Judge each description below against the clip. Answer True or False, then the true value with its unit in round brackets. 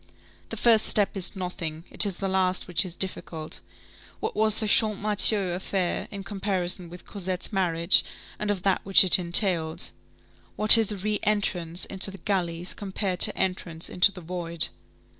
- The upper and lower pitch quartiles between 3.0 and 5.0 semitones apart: False (2.5 semitones)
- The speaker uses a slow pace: False (165 wpm)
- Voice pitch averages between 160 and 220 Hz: True (190 Hz)